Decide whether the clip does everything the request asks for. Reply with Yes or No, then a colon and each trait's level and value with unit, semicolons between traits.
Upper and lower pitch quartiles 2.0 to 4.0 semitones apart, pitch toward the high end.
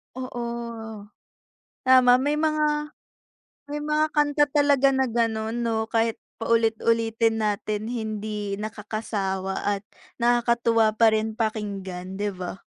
Yes: average, 3.3 semitones; high, 225 Hz